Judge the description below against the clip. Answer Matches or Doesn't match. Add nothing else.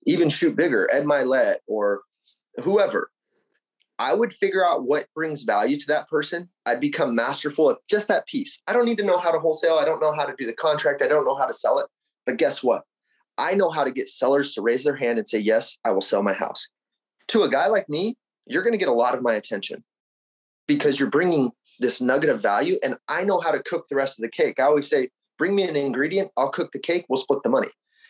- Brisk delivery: Matches